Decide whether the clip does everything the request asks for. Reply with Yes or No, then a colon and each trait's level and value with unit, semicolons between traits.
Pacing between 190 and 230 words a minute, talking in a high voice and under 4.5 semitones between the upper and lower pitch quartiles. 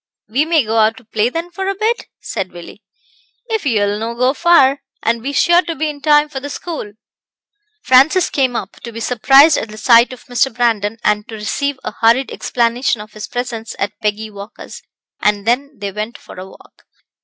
No: average, 200 wpm; high, 240 Hz; average, 4.8 semitones